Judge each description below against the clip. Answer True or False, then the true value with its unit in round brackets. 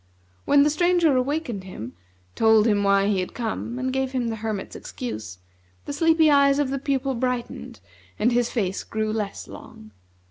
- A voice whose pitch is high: True (245 Hz)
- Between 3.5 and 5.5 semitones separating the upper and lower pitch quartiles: True (4.9 semitones)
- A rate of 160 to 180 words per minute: True (175 wpm)